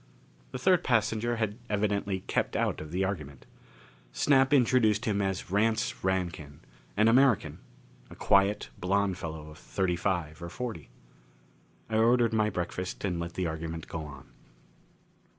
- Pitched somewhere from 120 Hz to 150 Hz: No, low, 100 Hz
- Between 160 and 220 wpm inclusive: No, average, 145 wpm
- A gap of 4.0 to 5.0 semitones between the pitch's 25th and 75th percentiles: Yes, average, 4.5 semitones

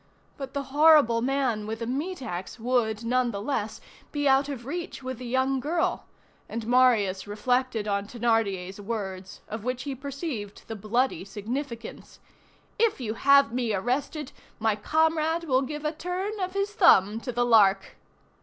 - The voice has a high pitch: Yes, very high, 250 Hz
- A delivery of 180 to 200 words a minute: No, average, 155 wpm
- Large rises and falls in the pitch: No, average, 4.5 semitones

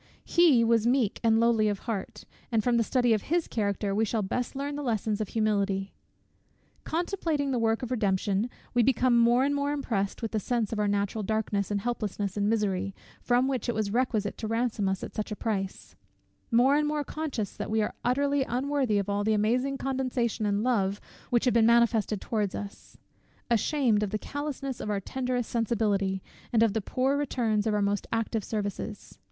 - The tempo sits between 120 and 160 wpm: No, average, 195 wpm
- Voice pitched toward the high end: Yes, high, 225 Hz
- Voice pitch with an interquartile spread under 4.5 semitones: Yes, average, 3.5 semitones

